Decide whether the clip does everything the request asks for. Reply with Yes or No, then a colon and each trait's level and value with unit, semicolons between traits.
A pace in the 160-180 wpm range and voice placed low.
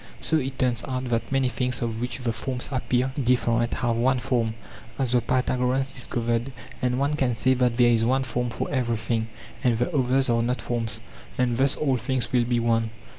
No: average, 200 wpm; low, 125 Hz